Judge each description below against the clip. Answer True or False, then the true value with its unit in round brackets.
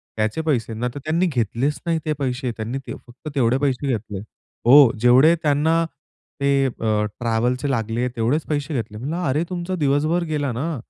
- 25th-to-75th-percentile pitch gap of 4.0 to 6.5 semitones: True (4.4 semitones)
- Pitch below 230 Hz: True (135 Hz)